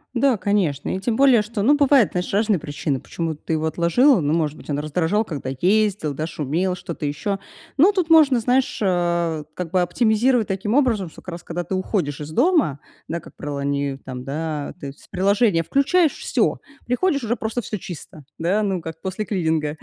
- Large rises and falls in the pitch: Yes, wide, 6.3 semitones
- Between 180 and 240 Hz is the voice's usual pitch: Yes, medium, 185 Hz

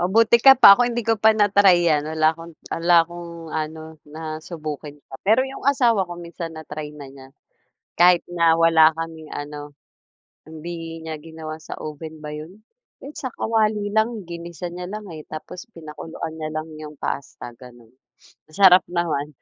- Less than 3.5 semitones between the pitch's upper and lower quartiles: Yes, average, 2.8 semitones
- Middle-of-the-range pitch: Yes, medium, 165 Hz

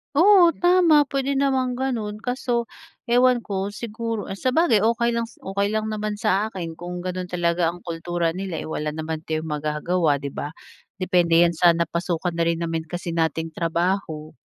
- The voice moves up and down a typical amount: No, wide, 5.9 semitones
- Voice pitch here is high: No, medium, 180 Hz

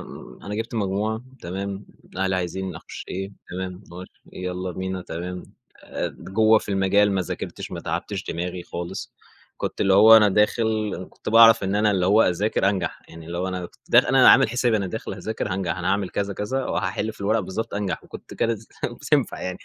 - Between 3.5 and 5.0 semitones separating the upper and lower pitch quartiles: No, average, 2.8 semitones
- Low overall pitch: Yes, very low, 95 Hz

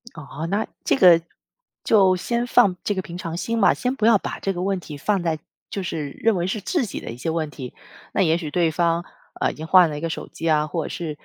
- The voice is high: No, medium, 175 Hz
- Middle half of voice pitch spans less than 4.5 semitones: Yes, average, 3.8 semitones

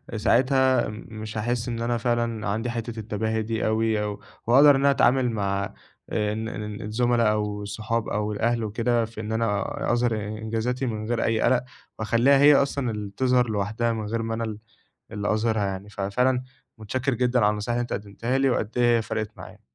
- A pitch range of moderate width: No, narrow, 2.2 semitones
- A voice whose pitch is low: Yes, low, 115 Hz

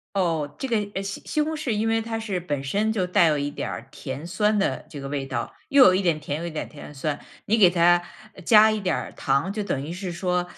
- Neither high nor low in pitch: Yes, medium, 180 Hz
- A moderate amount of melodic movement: No, wide, 5.9 semitones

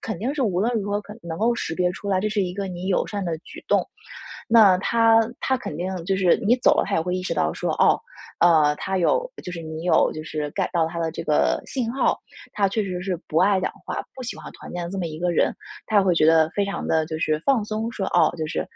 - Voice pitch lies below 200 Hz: Yes, medium, 185 Hz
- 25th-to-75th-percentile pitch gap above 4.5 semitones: No, average, 4.2 semitones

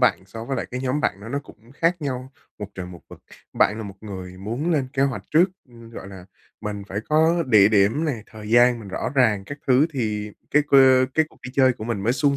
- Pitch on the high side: No, low, 120 Hz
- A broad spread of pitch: No, average, 4.8 semitones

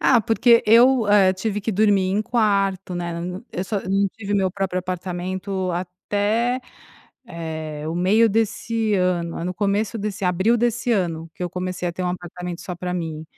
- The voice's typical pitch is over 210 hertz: No, high, 190 Hz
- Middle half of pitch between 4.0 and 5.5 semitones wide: No, average, 3.1 semitones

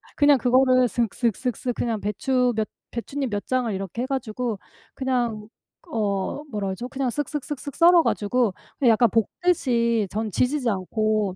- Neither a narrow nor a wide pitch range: Yes, average, 3.5 semitones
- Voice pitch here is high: Yes, high, 240 Hz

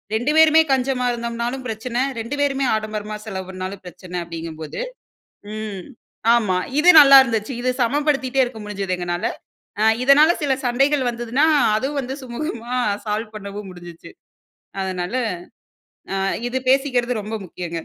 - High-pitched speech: Yes, high, 230 Hz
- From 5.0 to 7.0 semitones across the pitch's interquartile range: Yes, wide, 5.5 semitones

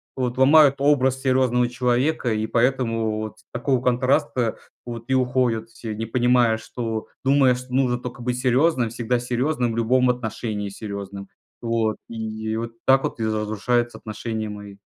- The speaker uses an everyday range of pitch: No, narrow, 2.3 semitones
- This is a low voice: Yes, low, 120 Hz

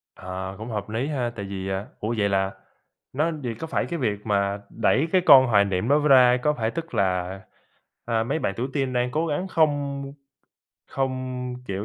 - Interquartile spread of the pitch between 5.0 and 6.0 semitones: Yes, wide, 5.6 semitones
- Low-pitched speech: Yes, low, 120 Hz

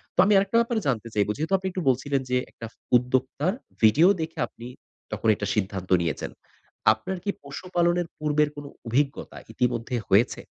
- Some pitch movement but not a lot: No, wide, 6.8 semitones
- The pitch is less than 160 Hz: Yes, medium, 140 Hz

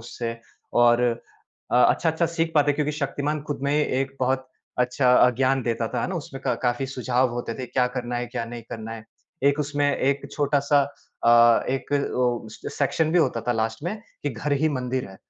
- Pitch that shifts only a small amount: No, average, 3.1 semitones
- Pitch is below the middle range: Yes, low, 130 Hz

